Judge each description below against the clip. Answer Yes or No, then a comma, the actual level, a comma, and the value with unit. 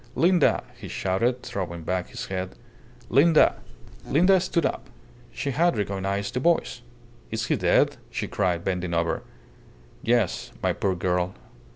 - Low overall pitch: Yes, low, 100 Hz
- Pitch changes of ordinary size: No, wide, 6.6 semitones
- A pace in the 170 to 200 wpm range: No, average, 140 wpm